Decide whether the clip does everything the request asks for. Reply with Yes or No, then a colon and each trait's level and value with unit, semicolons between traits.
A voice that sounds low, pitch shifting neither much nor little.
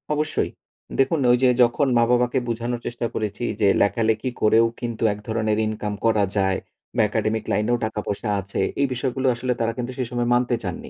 No: low, 115 Hz; narrow, 2.3 semitones